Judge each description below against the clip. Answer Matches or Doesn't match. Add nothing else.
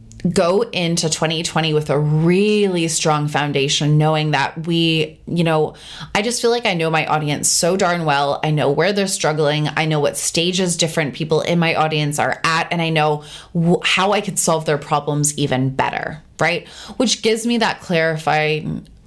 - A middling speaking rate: Matches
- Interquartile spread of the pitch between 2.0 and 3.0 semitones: Matches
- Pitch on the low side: Doesn't match